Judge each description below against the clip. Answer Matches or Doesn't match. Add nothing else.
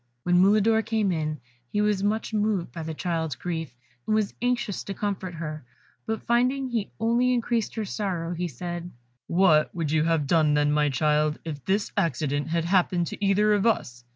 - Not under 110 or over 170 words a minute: Doesn't match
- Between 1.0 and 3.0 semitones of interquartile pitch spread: Doesn't match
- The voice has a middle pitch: Matches